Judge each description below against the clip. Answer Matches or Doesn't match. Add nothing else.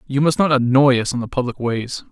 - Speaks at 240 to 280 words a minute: Matches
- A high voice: Doesn't match